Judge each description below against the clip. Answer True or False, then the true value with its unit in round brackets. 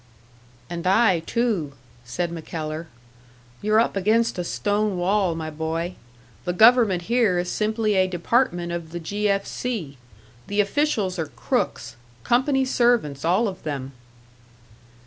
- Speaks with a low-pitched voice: False (185 Hz)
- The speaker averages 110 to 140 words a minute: True (135 wpm)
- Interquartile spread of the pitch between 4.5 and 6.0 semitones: True (4.9 semitones)